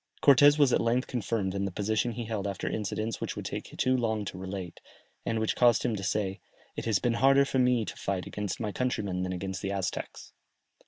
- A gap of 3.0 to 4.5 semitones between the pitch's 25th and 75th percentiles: Yes, average, 3.8 semitones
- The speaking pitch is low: Yes, low, 110 Hz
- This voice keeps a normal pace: No, fast, 220 wpm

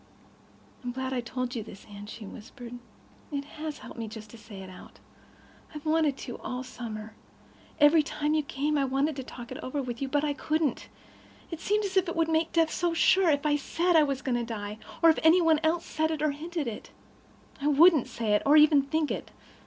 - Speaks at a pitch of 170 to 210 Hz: No, very high, 285 Hz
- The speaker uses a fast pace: Yes, fast, 225 wpm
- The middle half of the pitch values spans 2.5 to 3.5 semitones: No, average, 4.6 semitones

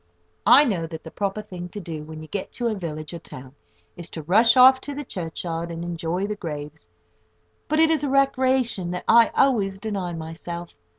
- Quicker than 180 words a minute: Yes, average, 200 wpm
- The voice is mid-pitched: Yes, medium, 180 Hz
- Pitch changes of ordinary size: No, wide, 6.2 semitones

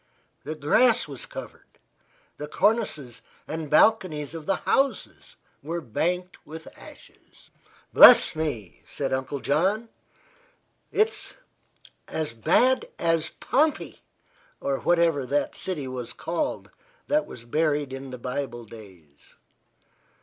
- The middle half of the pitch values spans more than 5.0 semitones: Yes, wide, 5.4 semitones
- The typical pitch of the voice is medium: Yes, medium, 150 Hz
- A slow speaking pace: Yes, slow, 115 wpm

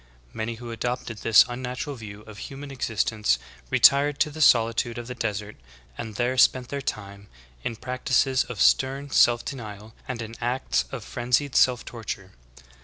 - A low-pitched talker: Yes, low, 120 Hz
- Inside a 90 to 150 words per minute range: No, average, 160 wpm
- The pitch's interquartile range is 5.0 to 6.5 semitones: No, average, 2.9 semitones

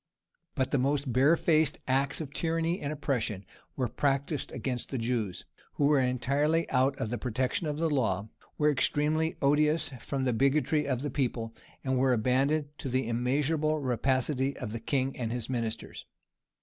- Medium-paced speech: Yes, average, 160 wpm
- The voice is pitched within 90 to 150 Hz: Yes, low, 135 Hz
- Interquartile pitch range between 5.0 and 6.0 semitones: No, average, 3.0 semitones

